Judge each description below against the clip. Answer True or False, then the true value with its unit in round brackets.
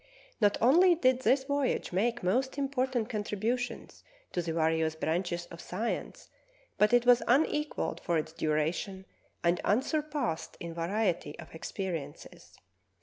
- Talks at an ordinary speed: False (130 wpm)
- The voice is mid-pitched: False (210 Hz)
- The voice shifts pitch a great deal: True (7.2 semitones)